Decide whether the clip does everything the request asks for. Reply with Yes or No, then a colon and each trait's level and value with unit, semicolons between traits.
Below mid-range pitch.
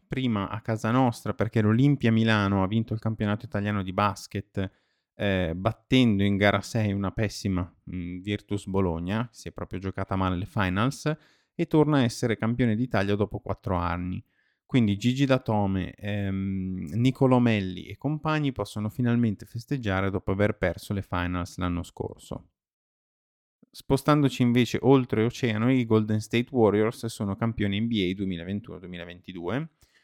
Yes: low, 105 Hz